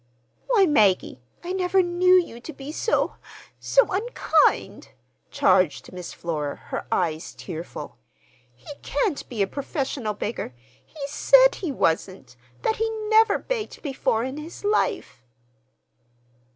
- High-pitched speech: Yes, very high, 280 Hz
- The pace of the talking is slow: Yes, slow, 120 wpm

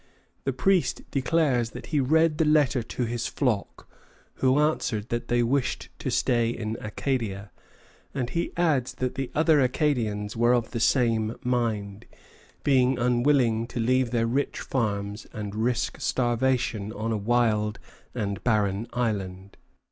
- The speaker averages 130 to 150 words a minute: Yes, average, 145 wpm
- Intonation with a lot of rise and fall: No, average, 3.2 semitones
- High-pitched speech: No, low, 120 Hz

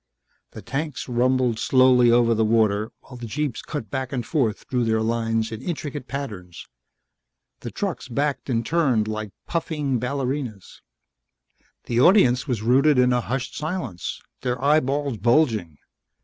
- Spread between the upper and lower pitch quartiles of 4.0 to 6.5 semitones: No, average, 3.6 semitones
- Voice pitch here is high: No, low, 125 Hz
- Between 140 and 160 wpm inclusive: Yes, average, 145 wpm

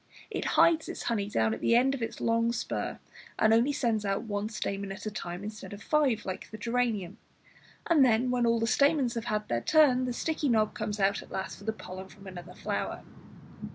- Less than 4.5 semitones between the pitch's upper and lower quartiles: Yes, average, 3.6 semitones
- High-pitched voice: Yes, high, 220 Hz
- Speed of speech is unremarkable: No, fast, 210 wpm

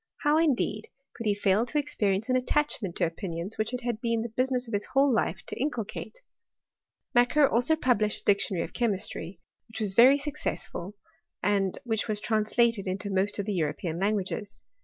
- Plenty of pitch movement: No, average, 4.0 semitones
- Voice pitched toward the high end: Yes, high, 215 Hz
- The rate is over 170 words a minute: Yes, average, 180 wpm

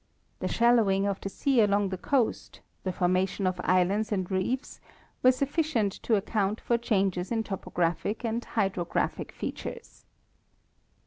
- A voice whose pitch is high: Yes, high, 200 Hz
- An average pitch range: Yes, average, 3.8 semitones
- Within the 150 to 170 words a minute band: No, average, 140 wpm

